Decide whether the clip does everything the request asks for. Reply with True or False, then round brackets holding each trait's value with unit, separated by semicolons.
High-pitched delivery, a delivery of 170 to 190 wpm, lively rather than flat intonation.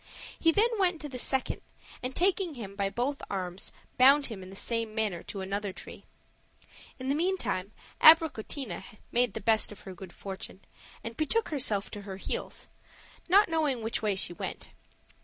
True (230 Hz; 175 wpm; 7.3 semitones)